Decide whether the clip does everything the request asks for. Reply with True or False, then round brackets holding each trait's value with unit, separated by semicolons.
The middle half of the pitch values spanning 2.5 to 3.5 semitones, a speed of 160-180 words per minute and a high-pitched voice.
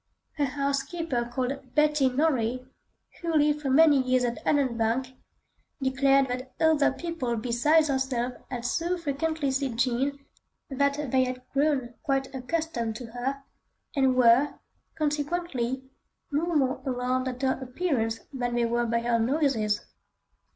False (2.9 semitones; 135 wpm; 265 Hz)